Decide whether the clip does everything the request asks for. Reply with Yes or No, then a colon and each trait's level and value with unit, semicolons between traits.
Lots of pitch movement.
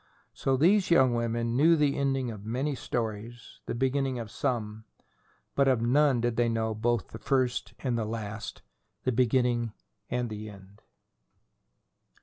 No: average, 2.9 semitones